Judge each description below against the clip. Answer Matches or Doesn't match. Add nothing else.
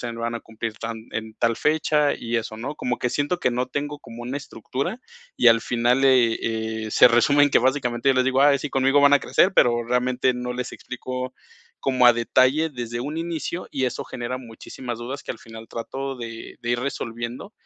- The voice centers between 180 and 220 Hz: Doesn't match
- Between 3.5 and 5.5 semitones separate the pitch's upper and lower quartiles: Doesn't match